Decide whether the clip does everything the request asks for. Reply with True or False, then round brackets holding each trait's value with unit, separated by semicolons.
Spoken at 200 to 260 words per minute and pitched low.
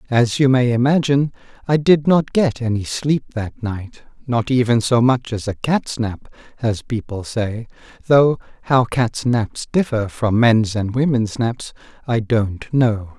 False (165 wpm; 120 Hz)